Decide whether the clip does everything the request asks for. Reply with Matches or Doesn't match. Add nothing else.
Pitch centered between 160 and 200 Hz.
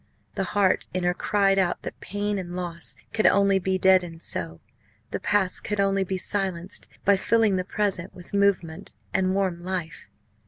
Matches